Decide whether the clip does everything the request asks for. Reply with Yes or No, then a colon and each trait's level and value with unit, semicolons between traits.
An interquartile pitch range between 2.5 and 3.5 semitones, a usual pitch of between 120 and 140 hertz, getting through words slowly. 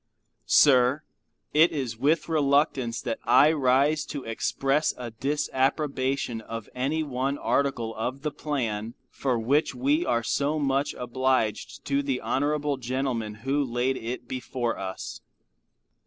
Yes: average, 3.2 semitones; low, 135 Hz; slow, 130 wpm